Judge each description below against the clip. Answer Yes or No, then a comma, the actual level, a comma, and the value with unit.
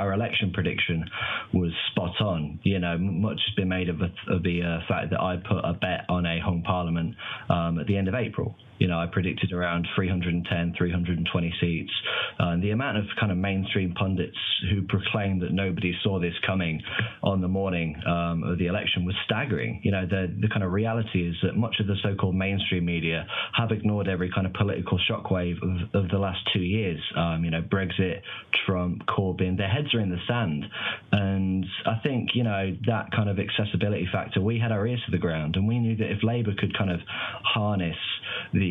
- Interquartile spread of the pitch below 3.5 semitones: Yes, average, 2.9 semitones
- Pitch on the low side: Yes, very low, 95 Hz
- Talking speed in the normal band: No, fast, 210 wpm